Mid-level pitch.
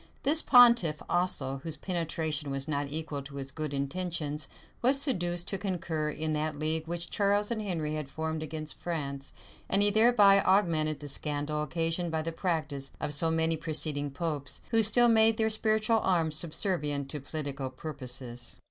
Yes: medium, 160 Hz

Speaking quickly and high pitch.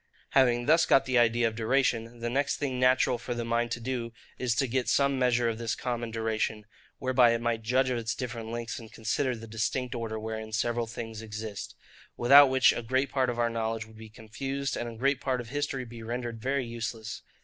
No: fast, 215 wpm; low, 120 Hz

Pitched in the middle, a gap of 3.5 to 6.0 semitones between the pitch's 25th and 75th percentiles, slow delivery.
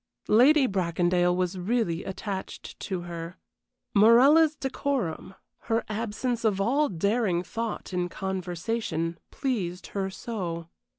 No: high, 195 Hz; average, 4.8 semitones; slow, 110 wpm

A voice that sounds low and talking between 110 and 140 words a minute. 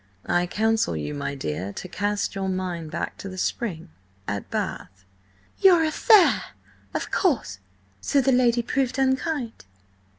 No: high, 195 Hz; slow, 135 wpm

